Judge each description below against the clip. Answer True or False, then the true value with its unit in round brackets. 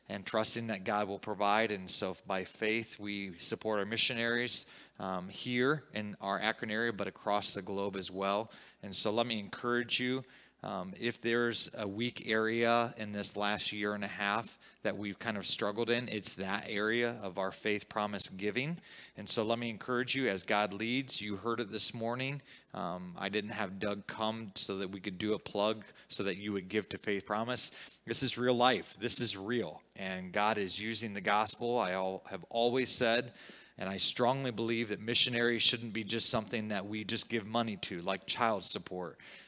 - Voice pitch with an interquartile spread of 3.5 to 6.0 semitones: False (2.6 semitones)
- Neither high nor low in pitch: False (110 Hz)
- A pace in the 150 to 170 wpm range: False (200 wpm)